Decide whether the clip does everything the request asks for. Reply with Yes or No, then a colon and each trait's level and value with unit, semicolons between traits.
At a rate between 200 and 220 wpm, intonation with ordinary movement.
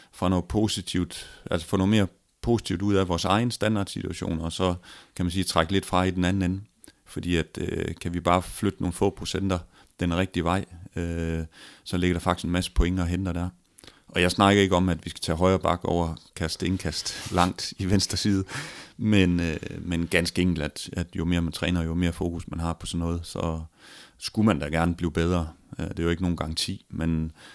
No: average, 215 wpm; narrow, 2.1 semitones